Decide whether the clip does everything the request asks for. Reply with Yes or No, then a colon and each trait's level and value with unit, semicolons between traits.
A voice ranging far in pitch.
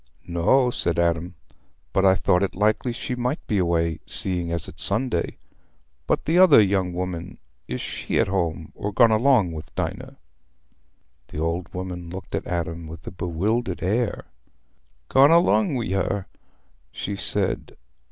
No: average, 4.6 semitones